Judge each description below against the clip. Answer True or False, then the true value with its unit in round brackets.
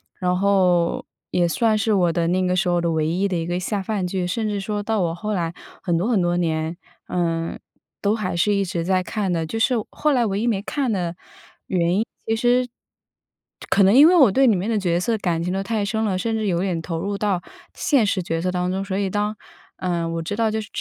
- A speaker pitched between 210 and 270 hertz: False (190 Hz)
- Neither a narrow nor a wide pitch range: True (3.5 semitones)